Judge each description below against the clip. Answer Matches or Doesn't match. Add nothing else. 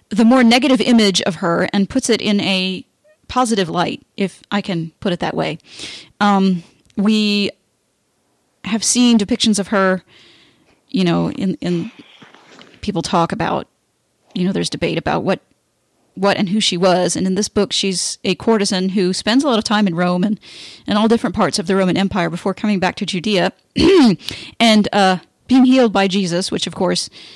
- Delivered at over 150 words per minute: Matches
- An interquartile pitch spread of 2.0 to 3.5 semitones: Matches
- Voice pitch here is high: Matches